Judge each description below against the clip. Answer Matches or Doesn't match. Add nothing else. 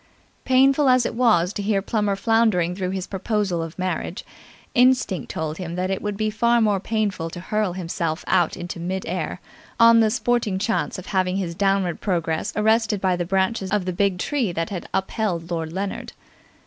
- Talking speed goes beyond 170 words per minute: Matches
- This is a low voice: Doesn't match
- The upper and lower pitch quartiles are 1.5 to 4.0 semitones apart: Matches